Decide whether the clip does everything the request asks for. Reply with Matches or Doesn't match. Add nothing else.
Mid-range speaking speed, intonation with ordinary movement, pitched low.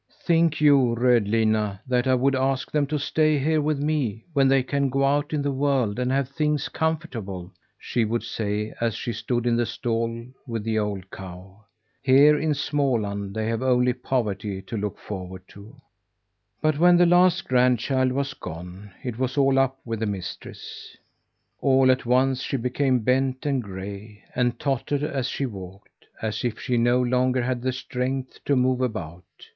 Matches